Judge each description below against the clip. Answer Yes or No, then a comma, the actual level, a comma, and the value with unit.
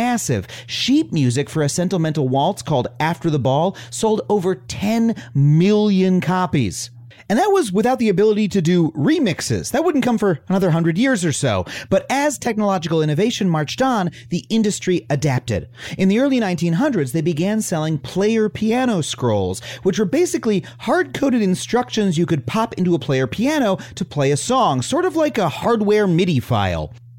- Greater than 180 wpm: No, average, 170 wpm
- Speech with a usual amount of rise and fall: No, wide, 7.3 semitones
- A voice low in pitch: No, medium, 185 Hz